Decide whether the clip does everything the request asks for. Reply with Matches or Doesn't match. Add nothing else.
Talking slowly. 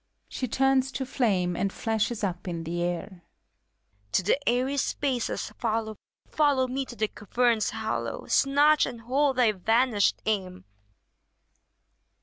Matches